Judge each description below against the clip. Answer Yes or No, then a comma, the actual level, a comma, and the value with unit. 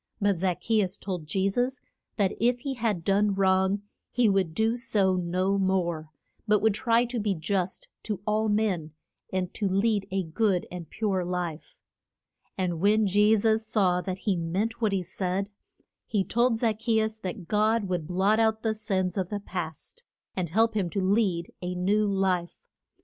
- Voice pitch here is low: No, high, 195 Hz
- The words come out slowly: No, average, 180 wpm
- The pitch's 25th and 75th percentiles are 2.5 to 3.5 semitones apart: Yes, average, 3.1 semitones